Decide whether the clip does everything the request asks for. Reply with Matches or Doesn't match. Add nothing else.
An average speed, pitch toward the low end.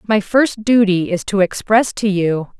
Doesn't match